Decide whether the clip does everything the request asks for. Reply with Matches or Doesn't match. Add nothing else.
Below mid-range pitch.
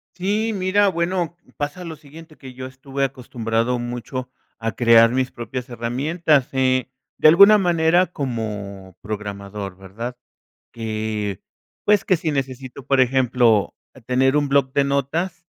Matches